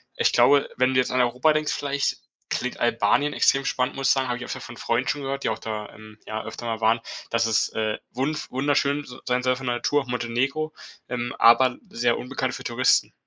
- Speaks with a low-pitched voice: Yes, low, 125 Hz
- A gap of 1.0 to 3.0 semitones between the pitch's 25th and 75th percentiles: Yes, narrow, 2.6 semitones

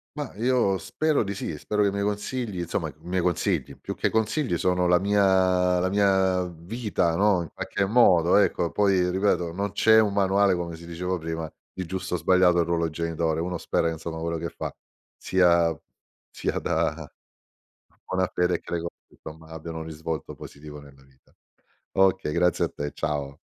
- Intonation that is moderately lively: Yes, average, 3.2 semitones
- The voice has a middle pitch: No, very low, 90 Hz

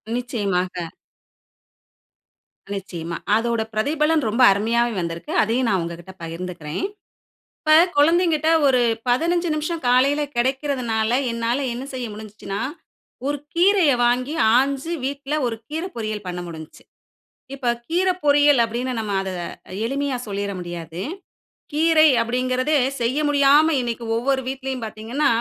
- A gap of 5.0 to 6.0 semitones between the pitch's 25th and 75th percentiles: Yes, wide, 5.5 semitones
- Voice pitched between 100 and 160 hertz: No, very high, 250 Hz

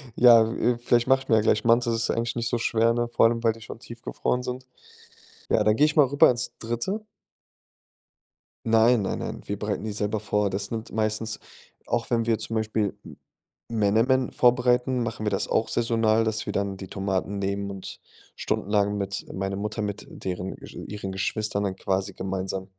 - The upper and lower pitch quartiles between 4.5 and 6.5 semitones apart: No, average, 2.8 semitones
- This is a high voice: No, low, 110 Hz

